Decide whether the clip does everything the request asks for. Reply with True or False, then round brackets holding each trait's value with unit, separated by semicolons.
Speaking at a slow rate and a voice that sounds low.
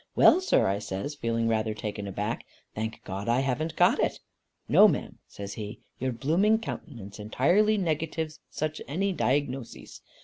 False (150 wpm; 125 Hz)